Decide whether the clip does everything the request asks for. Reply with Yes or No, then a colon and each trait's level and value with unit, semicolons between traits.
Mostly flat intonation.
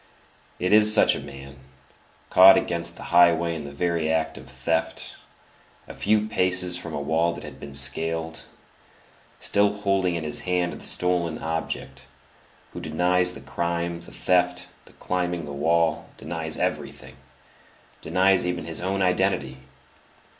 Yes: narrow, 2.3 semitones